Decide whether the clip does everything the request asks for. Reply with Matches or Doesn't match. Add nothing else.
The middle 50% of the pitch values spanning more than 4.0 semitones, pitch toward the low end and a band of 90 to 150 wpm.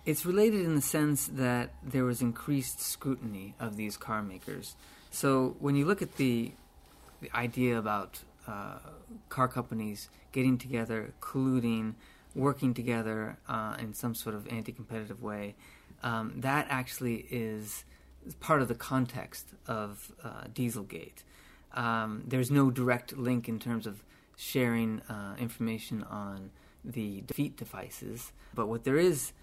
Doesn't match